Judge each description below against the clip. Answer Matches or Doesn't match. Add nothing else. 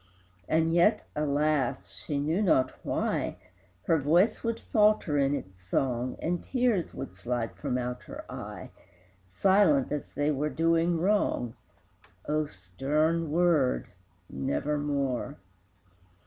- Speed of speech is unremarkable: Doesn't match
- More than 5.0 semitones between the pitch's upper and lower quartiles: Doesn't match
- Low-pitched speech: Doesn't match